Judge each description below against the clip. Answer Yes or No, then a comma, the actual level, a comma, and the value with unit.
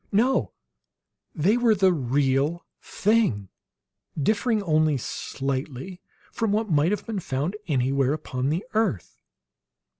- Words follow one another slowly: Yes, slow, 115 wpm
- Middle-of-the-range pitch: Yes, medium, 160 Hz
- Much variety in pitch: Yes, wide, 7.4 semitones